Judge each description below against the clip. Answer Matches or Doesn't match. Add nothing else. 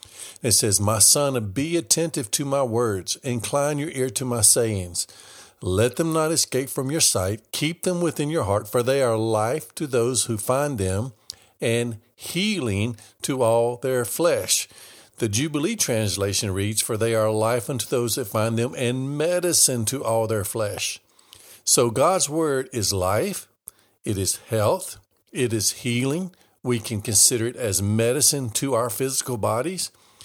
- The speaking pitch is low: Matches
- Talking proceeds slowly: Doesn't match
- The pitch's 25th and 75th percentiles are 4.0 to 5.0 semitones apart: Matches